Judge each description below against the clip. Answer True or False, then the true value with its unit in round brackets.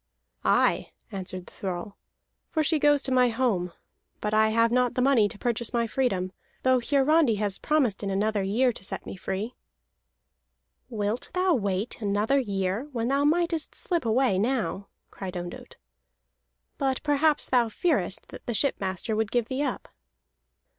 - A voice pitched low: False (230 Hz)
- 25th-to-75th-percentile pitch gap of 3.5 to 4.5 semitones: False (5.1 semitones)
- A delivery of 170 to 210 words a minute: False (160 wpm)